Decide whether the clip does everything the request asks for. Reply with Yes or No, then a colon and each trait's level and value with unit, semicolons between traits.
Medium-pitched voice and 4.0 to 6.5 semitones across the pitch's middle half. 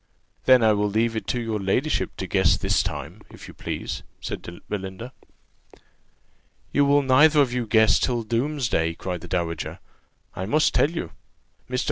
No: low, 115 Hz; average, 5.2 semitones